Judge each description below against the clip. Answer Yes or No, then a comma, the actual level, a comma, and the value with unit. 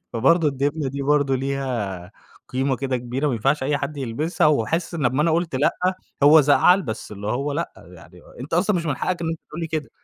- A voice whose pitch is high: No, medium, 140 Hz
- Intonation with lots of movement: No, average, 3.8 semitones